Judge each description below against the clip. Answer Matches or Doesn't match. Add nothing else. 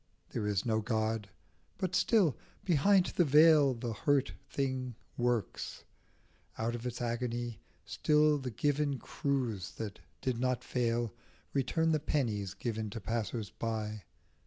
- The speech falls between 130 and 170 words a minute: Matches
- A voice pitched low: Matches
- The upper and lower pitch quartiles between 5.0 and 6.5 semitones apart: Doesn't match